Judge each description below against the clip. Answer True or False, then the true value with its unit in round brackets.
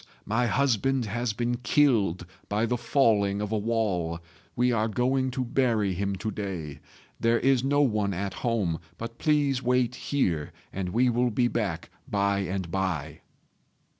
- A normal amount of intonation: True (4.0 semitones)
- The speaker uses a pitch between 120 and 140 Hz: False (110 Hz)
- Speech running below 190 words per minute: True (160 wpm)